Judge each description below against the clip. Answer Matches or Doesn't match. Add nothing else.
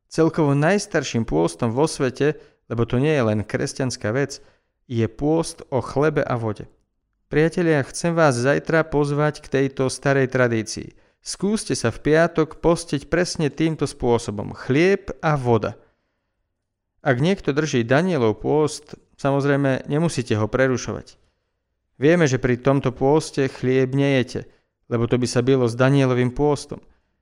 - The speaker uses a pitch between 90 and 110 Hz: Doesn't match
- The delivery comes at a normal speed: Matches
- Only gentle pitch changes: Doesn't match